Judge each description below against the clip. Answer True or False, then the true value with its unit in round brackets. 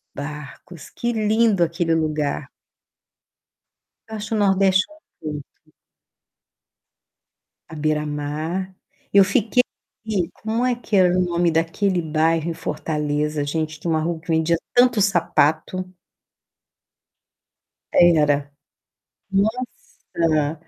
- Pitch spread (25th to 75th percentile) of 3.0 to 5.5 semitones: True (4.2 semitones)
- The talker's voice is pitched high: False (165 Hz)